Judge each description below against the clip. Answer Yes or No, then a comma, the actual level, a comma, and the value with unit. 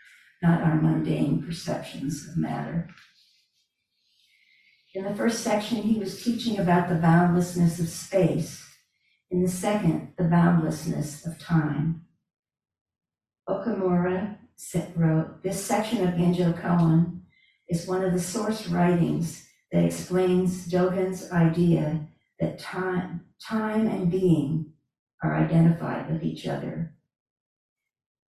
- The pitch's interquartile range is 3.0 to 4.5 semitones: No, narrow, 2.6 semitones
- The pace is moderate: No, slow, 110 wpm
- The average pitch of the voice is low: No, medium, 175 Hz